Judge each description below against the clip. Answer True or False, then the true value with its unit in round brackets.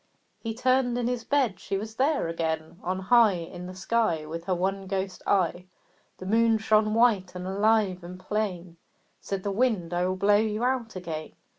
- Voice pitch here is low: False (195 Hz)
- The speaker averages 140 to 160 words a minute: False (185 wpm)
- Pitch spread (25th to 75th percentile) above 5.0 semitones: False (3.8 semitones)